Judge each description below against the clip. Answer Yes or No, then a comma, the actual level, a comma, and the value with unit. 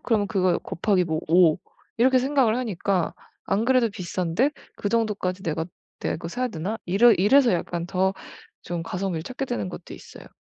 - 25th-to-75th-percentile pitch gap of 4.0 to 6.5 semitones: Yes, average, 5.1 semitones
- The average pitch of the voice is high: Yes, high, 195 Hz